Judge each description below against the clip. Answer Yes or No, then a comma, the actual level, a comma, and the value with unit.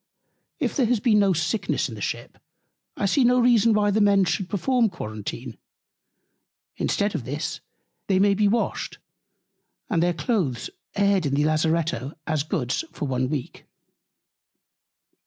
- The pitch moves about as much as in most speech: No, wide, 6.0 semitones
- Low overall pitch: No, medium, 185 Hz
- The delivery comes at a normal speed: Yes, average, 150 wpm